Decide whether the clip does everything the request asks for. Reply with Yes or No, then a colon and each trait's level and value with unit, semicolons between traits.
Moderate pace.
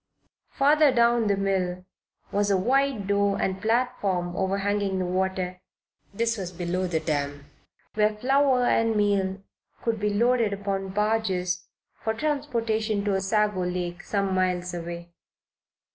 No: slow, 130 wpm